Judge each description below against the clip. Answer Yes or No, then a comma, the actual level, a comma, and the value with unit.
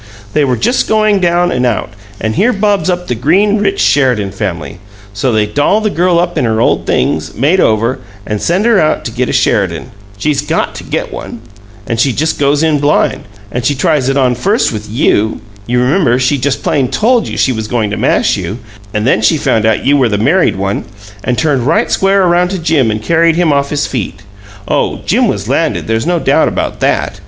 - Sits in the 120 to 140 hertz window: Yes, low, 135 Hz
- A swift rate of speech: Yes, fast, 220 wpm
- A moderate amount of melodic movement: No, wide, 7.5 semitones